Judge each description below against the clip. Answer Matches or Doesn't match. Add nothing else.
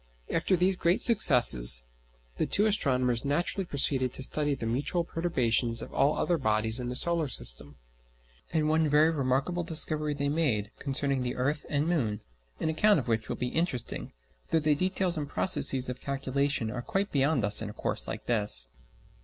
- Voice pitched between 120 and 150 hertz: Matches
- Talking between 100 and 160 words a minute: Doesn't match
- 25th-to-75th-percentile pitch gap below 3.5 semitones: Doesn't match